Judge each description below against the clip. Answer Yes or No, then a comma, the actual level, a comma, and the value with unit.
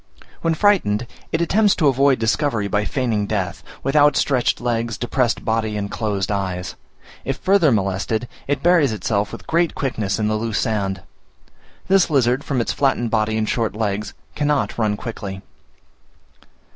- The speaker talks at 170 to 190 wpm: No, average, 155 wpm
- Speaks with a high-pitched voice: No, low, 115 Hz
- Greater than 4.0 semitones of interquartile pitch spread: Yes, average, 5.1 semitones